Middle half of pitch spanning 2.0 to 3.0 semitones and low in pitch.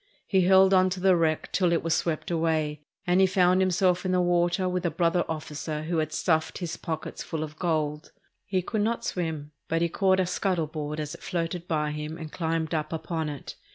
No: average, 2.7 semitones; medium, 170 Hz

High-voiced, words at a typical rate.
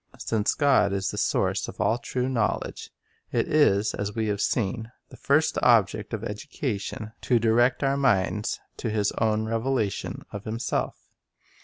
No: low, 110 Hz; average, 160 wpm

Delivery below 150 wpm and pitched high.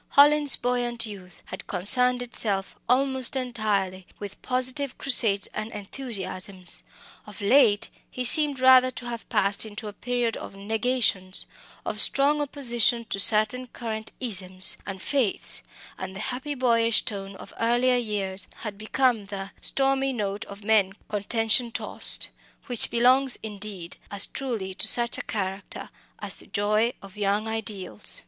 Yes: average, 140 wpm; high, 220 Hz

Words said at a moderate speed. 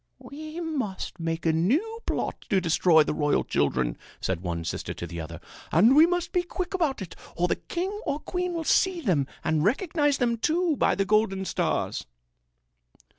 Yes: average, 180 wpm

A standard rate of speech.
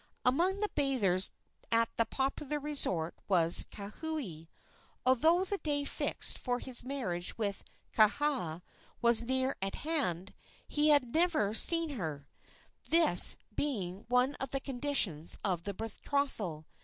No: slow, 130 wpm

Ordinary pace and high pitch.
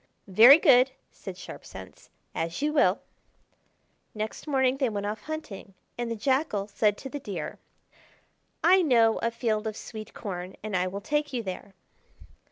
Yes: average, 165 wpm; high, 225 Hz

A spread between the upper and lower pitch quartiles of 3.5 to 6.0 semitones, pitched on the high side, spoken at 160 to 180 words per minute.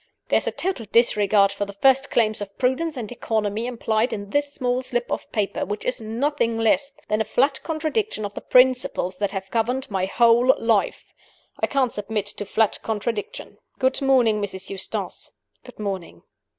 Yes: average, 4.0 semitones; high, 225 Hz; average, 175 wpm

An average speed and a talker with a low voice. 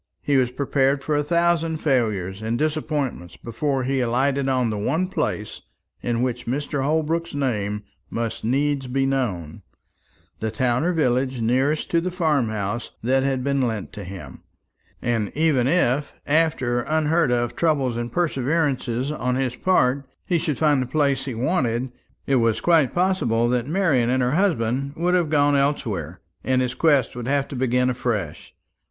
Yes: average, 165 wpm; low, 130 Hz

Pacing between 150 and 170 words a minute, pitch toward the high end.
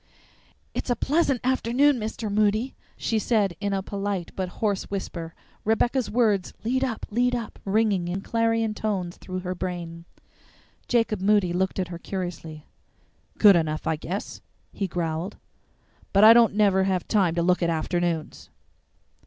Yes: average, 155 wpm; high, 200 Hz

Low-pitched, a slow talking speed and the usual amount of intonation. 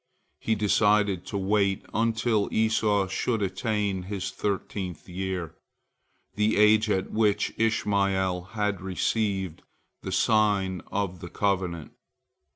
No: low, 100 Hz; slow, 110 wpm; narrow, 2.1 semitones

